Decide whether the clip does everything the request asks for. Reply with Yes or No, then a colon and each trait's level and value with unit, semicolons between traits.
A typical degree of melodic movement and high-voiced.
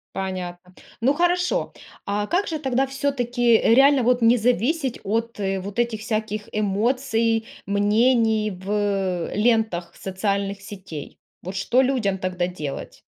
Yes: average, 4.2 semitones; high, 220 Hz